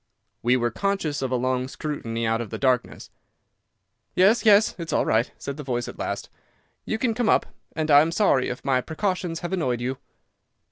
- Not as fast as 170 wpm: No, average, 195 wpm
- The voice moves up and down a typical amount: No, wide, 6.6 semitones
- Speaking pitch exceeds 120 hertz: Yes, medium, 140 Hz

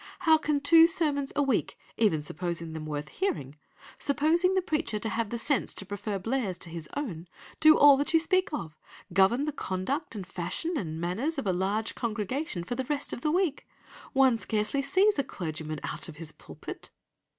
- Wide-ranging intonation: Yes, wide, 8.7 semitones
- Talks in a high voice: Yes, high, 235 Hz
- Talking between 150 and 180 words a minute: No, average, 195 wpm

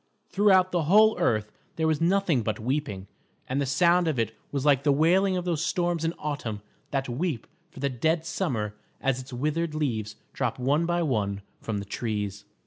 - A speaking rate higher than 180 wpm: Yes, average, 190 wpm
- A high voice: No, medium, 145 Hz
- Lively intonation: Yes, wide, 6.6 semitones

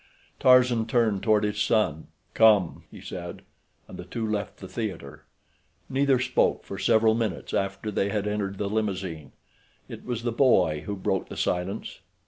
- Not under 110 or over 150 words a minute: No, average, 160 wpm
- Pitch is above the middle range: No, low, 105 Hz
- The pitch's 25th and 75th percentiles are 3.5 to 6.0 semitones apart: No, average, 2.9 semitones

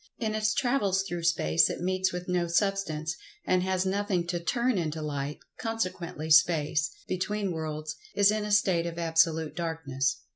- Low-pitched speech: No, medium, 175 Hz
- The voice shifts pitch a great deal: No, average, 3.6 semitones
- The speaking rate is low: No, average, 155 wpm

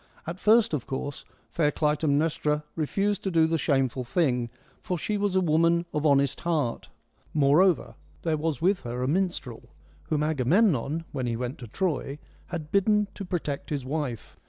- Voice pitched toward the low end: No, medium, 155 Hz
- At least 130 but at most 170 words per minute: No, average, 180 wpm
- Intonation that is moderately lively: Yes, average, 4.3 semitones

